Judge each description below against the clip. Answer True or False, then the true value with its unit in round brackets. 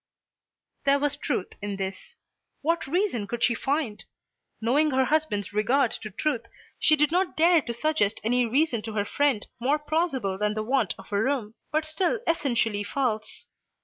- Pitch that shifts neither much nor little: False (6.1 semitones)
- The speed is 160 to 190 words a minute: True (170 wpm)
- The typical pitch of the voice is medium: False (255 Hz)